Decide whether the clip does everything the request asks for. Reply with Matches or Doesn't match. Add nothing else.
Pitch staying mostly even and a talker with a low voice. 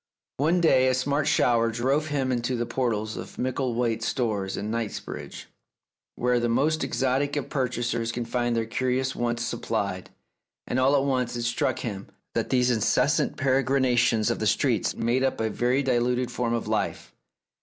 Matches